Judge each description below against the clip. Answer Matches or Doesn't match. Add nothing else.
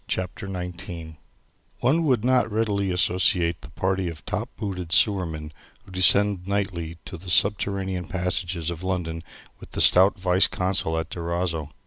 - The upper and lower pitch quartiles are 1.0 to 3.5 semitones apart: Matches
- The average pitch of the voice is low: Matches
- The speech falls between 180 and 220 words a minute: Doesn't match